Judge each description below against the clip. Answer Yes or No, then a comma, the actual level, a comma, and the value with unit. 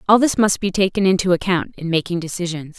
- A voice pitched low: No, medium, 180 Hz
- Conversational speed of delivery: No, fast, 215 wpm